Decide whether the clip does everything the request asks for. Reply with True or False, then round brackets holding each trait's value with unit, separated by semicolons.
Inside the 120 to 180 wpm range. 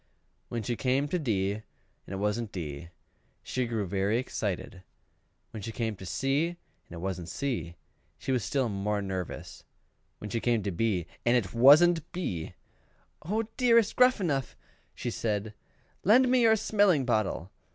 True (160 wpm)